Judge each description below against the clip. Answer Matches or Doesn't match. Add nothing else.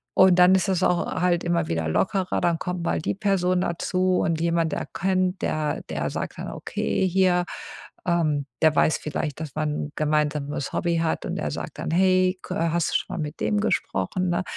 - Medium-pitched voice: Matches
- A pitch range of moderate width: Matches